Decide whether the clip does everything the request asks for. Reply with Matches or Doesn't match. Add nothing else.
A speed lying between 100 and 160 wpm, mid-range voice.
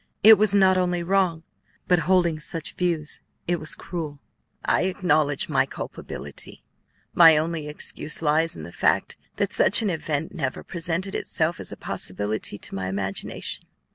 Matches